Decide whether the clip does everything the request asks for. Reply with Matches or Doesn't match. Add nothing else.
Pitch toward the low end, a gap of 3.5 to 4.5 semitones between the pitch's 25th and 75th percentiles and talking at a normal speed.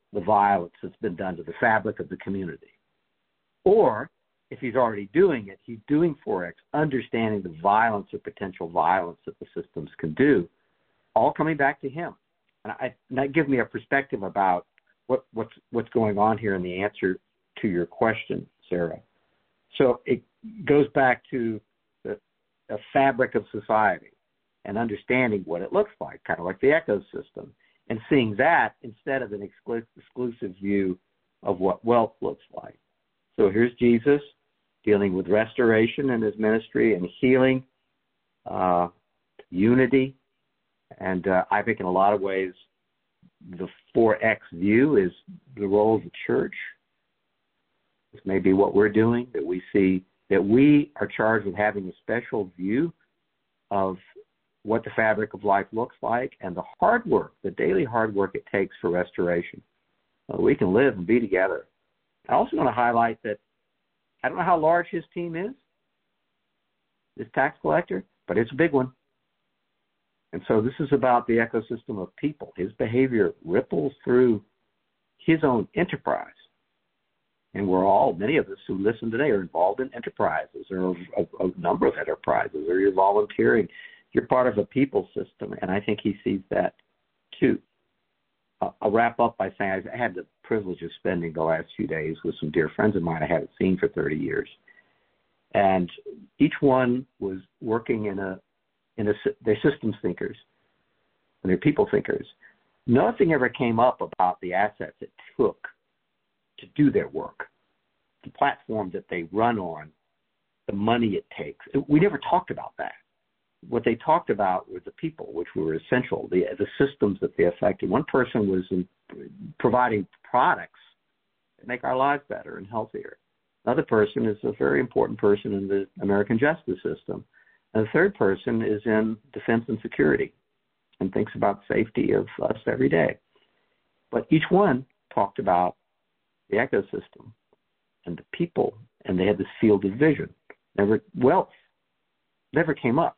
Doesn't match